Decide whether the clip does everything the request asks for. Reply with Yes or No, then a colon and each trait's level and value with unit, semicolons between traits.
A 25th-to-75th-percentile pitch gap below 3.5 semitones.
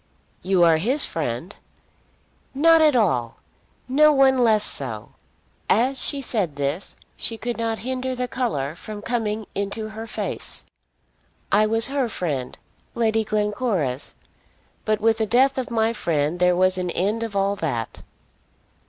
No: wide, 5.4 semitones